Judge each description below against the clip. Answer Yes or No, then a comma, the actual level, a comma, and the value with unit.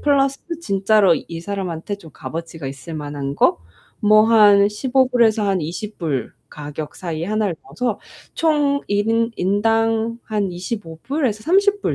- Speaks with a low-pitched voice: No, high, 205 Hz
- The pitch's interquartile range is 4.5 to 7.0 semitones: Yes, wide, 5.6 semitones